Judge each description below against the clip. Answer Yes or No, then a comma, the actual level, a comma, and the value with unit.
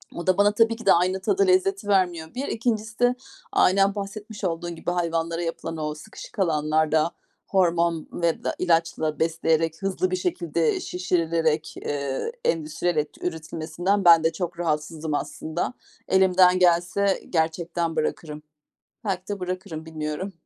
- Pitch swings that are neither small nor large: Yes, average, 3.0 semitones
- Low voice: No, medium, 170 Hz